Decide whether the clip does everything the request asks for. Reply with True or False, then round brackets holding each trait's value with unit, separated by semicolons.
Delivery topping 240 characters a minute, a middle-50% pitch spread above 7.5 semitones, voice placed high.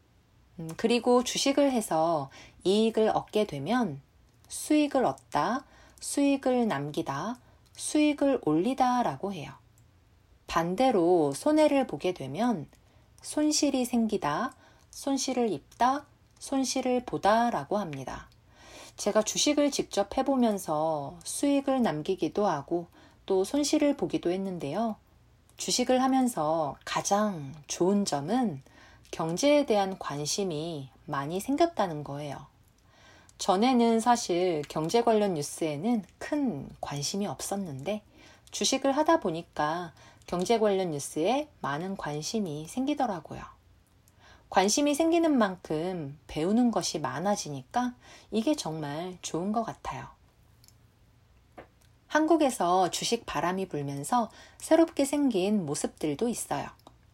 False (235 characters per minute; 8.5 semitones; 195 Hz)